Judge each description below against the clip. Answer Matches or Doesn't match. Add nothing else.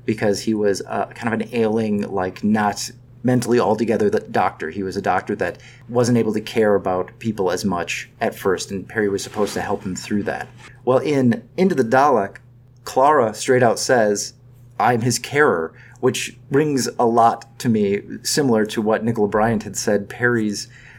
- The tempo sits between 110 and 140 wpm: Doesn't match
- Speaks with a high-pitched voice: Doesn't match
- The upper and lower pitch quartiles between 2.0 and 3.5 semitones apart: Matches